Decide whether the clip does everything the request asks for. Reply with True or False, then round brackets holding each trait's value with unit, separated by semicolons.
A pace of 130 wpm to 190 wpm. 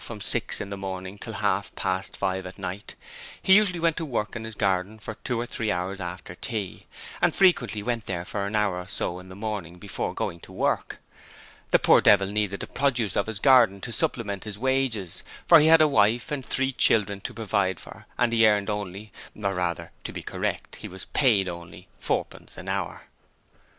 False (205 wpm)